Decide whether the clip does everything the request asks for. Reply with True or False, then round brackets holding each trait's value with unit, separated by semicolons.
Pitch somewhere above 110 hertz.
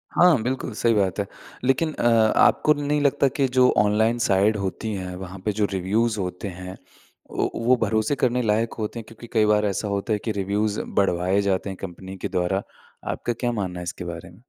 False (105 Hz)